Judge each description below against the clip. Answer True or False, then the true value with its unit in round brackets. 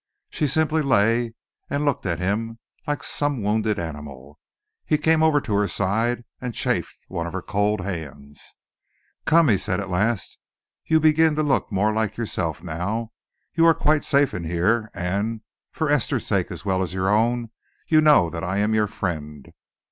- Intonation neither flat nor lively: False (7.4 semitones)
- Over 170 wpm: True (180 wpm)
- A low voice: True (110 Hz)